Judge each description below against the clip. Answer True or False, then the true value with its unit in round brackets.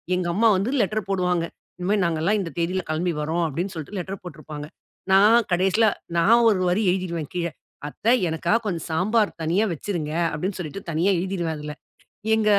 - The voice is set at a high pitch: False (180 Hz)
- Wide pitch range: False (3.5 semitones)